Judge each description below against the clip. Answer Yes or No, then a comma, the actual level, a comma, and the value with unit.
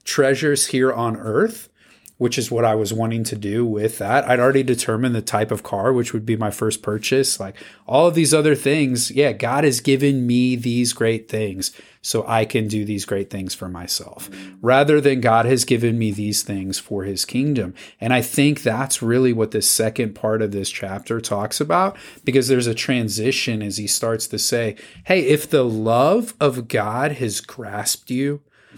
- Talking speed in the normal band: Yes, average, 195 wpm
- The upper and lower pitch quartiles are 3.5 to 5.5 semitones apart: Yes, average, 3.8 semitones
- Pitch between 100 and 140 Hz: Yes, low, 115 Hz